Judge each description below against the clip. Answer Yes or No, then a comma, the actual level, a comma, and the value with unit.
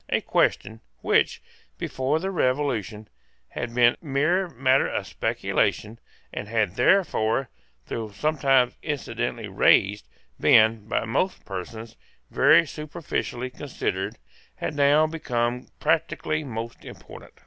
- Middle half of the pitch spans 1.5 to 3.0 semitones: No, average, 5.1 semitones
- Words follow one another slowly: Yes, slow, 110 wpm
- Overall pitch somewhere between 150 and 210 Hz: No, low, 130 Hz